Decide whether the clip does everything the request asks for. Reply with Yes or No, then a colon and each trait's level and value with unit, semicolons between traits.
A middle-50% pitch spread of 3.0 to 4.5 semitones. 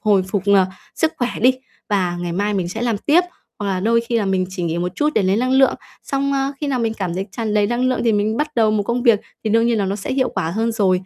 Yes: average, 4.0 semitones